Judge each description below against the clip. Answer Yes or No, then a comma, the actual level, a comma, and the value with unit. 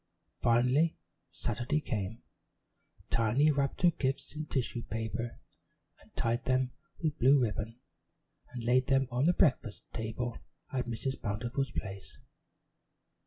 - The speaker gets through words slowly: Yes, slow, 120 wpm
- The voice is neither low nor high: No, low, 125 Hz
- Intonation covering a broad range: No, average, 3.0 semitones